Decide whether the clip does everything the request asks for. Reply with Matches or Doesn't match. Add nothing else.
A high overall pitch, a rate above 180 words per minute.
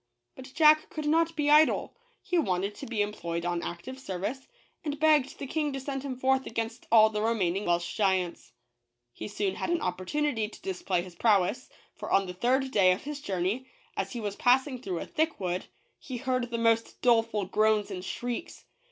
Matches